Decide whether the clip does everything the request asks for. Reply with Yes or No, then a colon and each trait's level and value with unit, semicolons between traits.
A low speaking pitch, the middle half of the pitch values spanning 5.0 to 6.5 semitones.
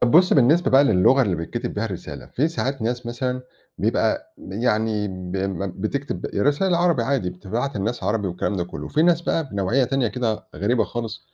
Yes: low, 120 Hz; wide, 5.4 semitones